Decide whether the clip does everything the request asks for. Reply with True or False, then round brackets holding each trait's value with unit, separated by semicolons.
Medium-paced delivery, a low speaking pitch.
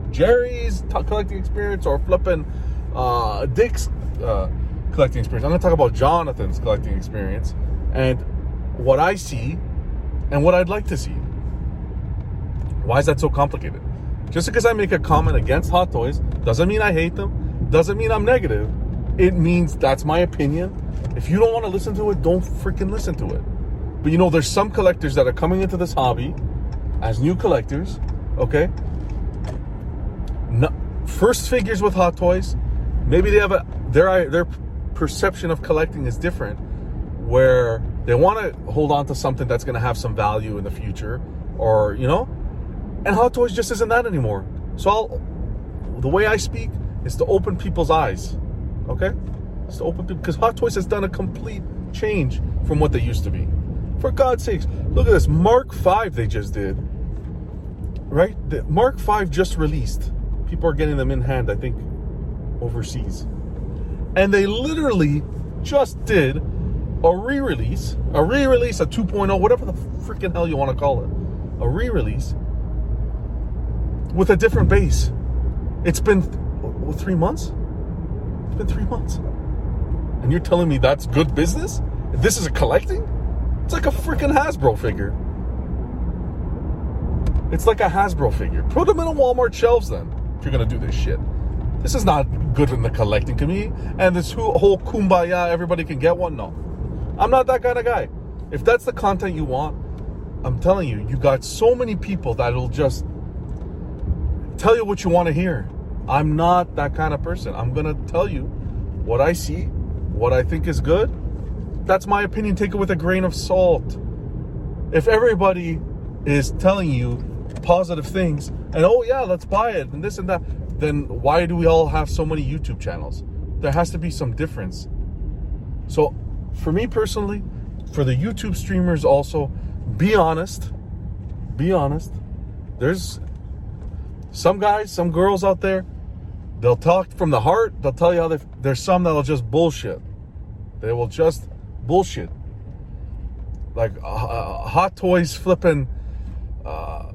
True (170 wpm; 120 Hz)